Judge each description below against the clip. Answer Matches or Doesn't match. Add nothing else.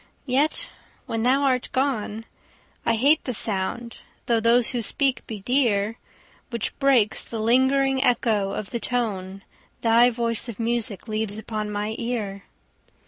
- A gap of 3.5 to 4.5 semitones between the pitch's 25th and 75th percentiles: Doesn't match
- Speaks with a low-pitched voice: Doesn't match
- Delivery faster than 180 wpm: Doesn't match